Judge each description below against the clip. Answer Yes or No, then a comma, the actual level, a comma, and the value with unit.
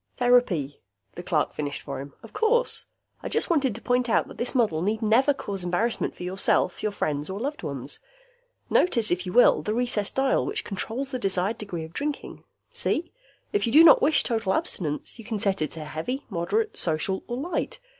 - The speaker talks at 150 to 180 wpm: No, average, 200 wpm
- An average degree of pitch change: No, wide, 6.3 semitones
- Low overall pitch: No, high, 215 Hz